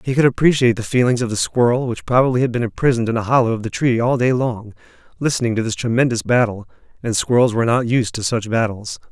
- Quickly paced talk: Yes, fast, 230 wpm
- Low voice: Yes, low, 120 Hz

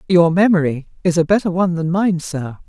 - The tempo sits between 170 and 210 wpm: Yes, average, 200 wpm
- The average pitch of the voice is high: No, medium, 170 Hz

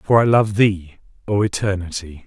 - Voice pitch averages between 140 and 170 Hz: No, low, 100 Hz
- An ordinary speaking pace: Yes, average, 160 wpm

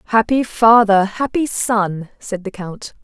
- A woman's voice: Yes, female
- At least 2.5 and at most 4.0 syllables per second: Yes, 3.8 syllables/s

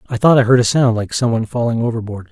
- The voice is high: No, low, 120 Hz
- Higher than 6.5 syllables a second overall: Yes, 7.1 syllables/s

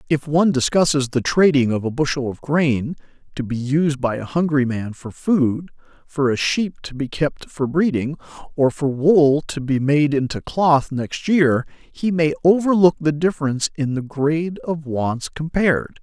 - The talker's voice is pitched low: No, medium, 145 Hz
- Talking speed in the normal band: Yes, average, 180 wpm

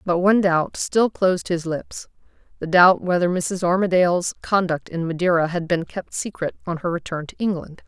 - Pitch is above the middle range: No, medium, 175 Hz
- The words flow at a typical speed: Yes, average, 175 wpm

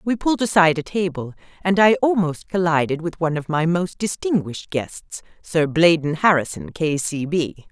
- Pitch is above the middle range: No, medium, 170 Hz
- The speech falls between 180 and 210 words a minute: No, average, 165 wpm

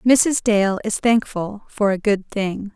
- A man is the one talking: No, female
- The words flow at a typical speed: Yes, average, 175 wpm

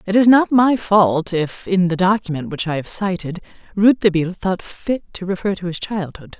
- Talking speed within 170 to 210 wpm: Yes, average, 195 wpm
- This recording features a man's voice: No, female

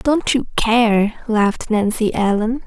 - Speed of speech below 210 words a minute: Yes, slow, 135 wpm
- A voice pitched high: Yes, high, 225 Hz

